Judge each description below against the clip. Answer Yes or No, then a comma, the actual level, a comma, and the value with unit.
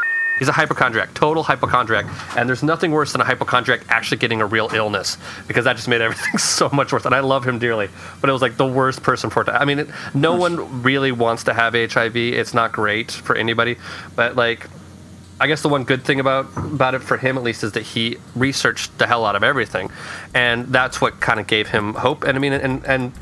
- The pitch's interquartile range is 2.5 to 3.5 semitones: Yes, average, 2.8 semitones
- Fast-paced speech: Yes, fast, 235 wpm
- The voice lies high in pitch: No, low, 130 Hz